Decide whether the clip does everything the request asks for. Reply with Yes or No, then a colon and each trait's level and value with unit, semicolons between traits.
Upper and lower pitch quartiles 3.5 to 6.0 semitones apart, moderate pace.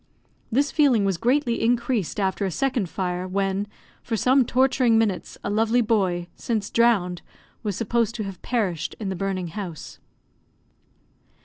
Yes: average, 3.9 semitones; average, 145 wpm